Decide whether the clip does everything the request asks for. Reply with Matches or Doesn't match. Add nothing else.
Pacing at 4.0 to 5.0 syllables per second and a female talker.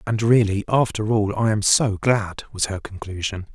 Doesn't match